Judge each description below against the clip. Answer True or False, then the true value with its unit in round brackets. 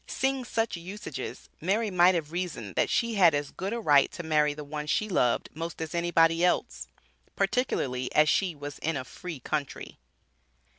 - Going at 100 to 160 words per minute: False (180 wpm)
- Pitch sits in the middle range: True (165 Hz)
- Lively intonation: False (4.2 semitones)